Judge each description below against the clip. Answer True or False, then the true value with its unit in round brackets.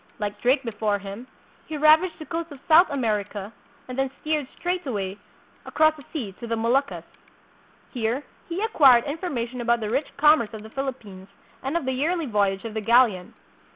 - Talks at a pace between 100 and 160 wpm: False (180 wpm)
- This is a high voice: True (255 Hz)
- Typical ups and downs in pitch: False (5.8 semitones)